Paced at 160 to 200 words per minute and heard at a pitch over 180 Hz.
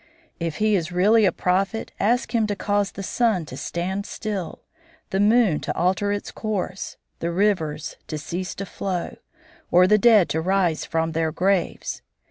Yes: average, 170 wpm; high, 190 Hz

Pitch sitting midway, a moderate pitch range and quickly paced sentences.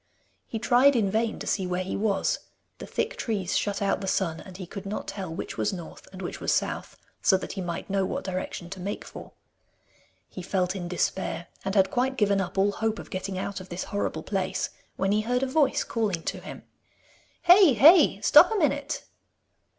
No: high, 195 Hz; average, 3.4 semitones; fast, 210 wpm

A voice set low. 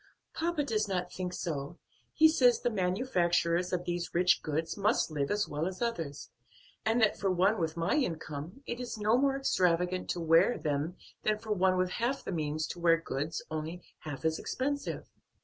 No: medium, 180 Hz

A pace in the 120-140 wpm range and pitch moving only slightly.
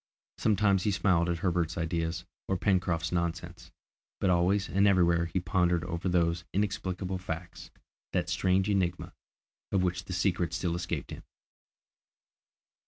Yes: slow, 135 wpm; narrow, 1.8 semitones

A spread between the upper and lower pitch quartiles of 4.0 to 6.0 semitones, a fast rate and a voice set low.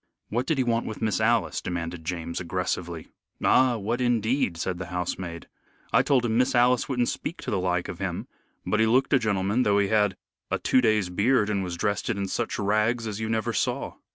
Yes: average, 4.5 semitones; fast, 210 wpm; low, 105 Hz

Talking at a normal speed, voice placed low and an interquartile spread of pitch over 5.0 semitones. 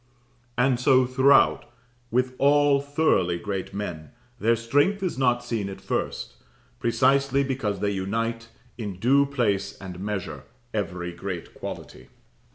No: slow, 130 wpm; low, 115 Hz; wide, 5.6 semitones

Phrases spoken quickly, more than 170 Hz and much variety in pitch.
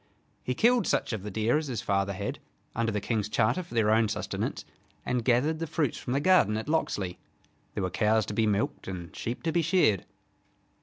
No: fast, 210 wpm; low, 115 Hz; wide, 6.3 semitones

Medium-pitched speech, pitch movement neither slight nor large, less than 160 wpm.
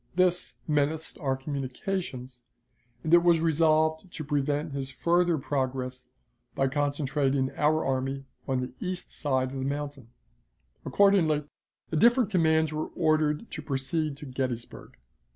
Yes: medium, 150 Hz; average, 3.1 semitones; slow, 135 wpm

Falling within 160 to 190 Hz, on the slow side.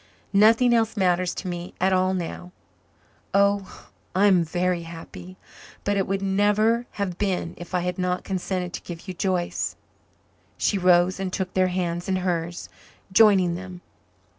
No: medium, 185 Hz; average, 160 wpm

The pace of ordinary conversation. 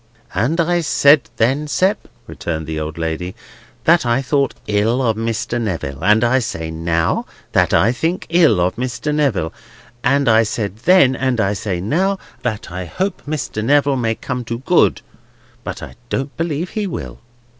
Yes: average, 170 wpm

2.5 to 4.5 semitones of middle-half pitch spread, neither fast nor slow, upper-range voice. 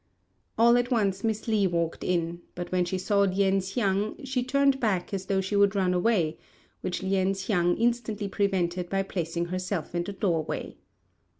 Yes: average, 2.9 semitones; average, 175 wpm; high, 195 Hz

